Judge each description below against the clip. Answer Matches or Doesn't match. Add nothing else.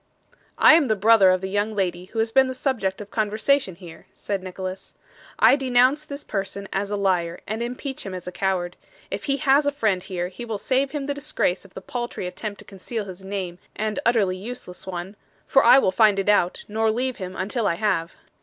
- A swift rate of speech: Matches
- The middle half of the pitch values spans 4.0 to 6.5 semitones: Matches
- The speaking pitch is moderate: Doesn't match